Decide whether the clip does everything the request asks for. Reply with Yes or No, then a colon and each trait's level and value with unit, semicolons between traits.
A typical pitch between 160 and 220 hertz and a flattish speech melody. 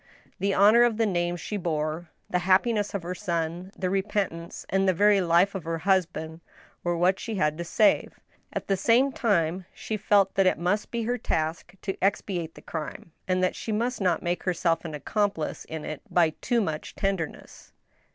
No: medium, 185 Hz; average, 3.4 semitones